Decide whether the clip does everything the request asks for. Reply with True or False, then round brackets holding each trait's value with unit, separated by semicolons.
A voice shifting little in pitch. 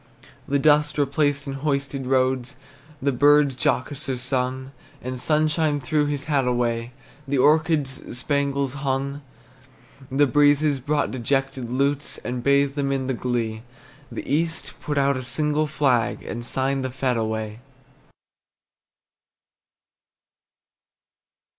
True (2.2 semitones)